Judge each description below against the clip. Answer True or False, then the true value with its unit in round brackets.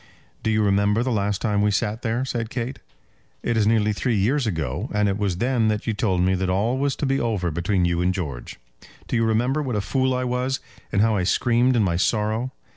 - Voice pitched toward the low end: True (110 Hz)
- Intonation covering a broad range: False (3.7 semitones)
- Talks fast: True (235 wpm)